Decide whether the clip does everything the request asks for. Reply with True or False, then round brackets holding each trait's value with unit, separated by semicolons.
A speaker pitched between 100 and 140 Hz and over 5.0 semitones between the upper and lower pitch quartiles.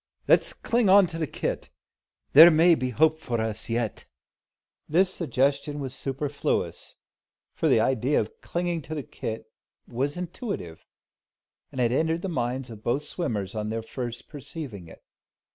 True (135 Hz; 5.6 semitones)